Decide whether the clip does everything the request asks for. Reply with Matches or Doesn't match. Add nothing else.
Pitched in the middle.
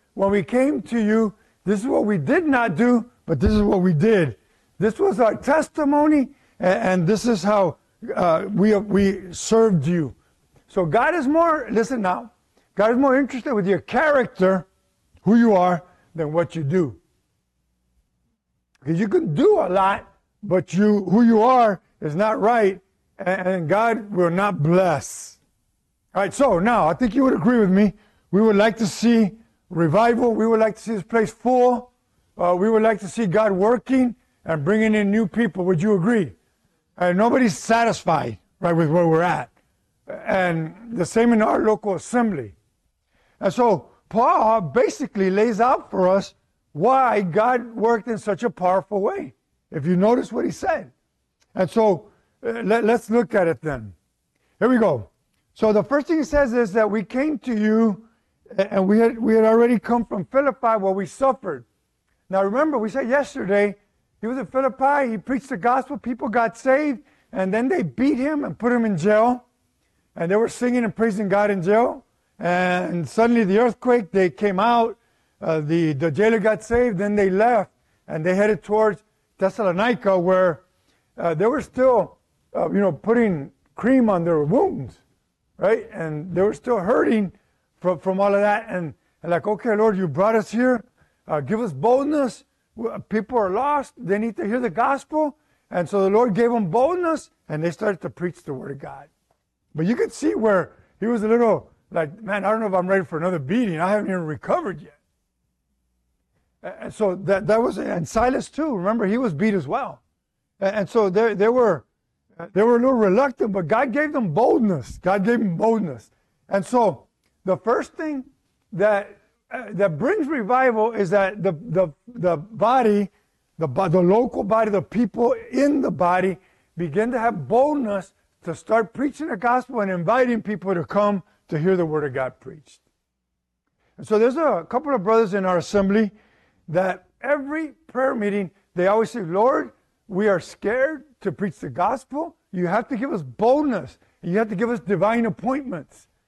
Doesn't match